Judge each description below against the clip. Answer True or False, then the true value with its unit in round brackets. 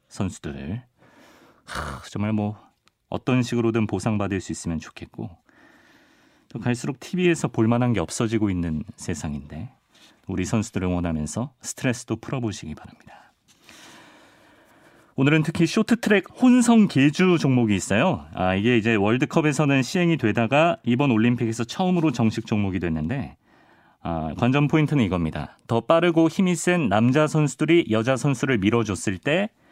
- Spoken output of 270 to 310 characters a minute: False (320 characters per minute)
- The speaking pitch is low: True (120 Hz)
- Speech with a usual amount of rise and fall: False (7.5 semitones)